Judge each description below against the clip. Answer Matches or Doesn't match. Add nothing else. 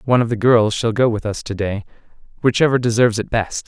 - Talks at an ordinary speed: Doesn't match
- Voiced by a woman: Doesn't match